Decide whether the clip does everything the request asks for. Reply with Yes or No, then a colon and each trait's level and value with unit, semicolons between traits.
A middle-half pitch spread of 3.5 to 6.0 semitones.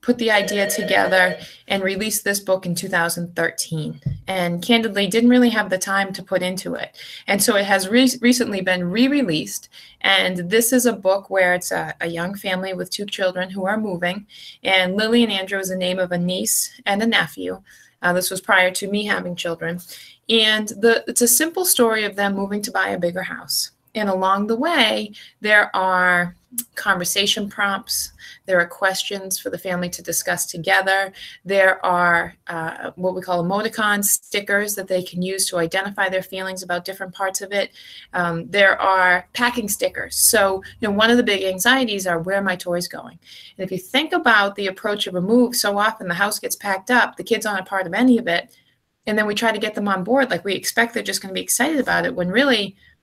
No: average, 2.8 semitones